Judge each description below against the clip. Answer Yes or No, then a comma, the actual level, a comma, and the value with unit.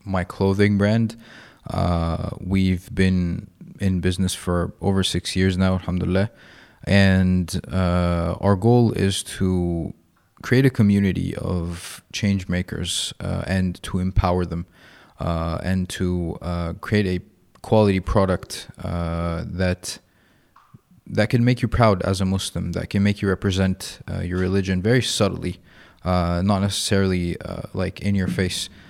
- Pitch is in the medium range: No, very low, 95 Hz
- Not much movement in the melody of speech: Yes, narrow, 2.1 semitones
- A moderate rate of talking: No, fast, 140 wpm